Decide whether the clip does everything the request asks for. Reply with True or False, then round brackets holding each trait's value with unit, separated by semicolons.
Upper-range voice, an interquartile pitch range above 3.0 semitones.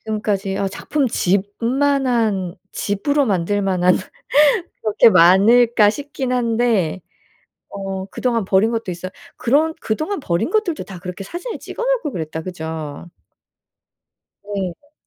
True (210 Hz; 5.4 semitones)